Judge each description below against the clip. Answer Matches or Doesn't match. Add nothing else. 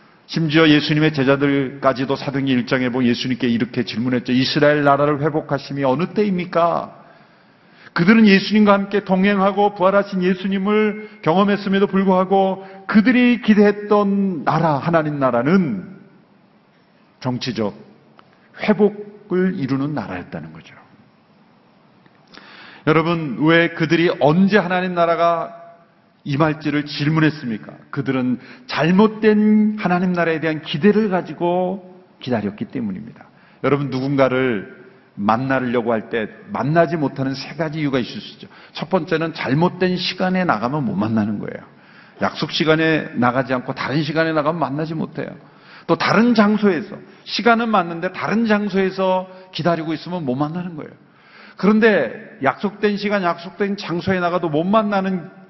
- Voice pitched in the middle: Matches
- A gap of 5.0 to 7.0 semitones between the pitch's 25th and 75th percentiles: Matches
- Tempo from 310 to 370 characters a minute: Matches